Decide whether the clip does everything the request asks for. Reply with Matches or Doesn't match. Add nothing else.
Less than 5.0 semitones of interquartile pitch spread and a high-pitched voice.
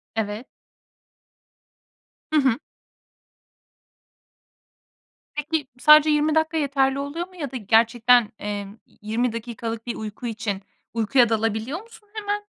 Doesn't match